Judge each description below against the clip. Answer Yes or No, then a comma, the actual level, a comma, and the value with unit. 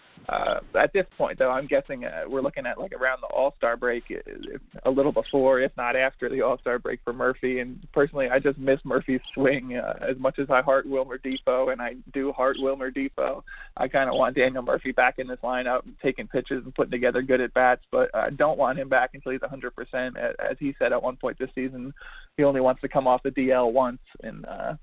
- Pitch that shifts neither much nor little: No, narrow, 1.2 semitones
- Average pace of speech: No, fast, 235 wpm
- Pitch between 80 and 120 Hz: No, low, 130 Hz